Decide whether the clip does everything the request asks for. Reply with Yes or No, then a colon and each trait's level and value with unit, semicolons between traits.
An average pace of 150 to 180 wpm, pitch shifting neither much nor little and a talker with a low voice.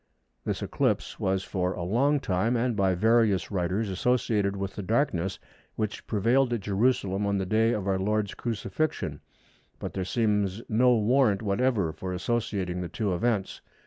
Yes: average, 160 wpm; average, 3.5 semitones; low, 105 Hz